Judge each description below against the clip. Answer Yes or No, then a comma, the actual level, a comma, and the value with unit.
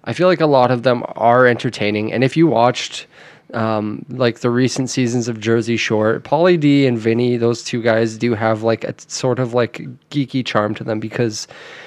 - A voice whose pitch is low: Yes, low, 120 Hz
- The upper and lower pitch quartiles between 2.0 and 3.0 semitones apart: Yes, narrow, 2.6 semitones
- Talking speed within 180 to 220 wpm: Yes, average, 200 wpm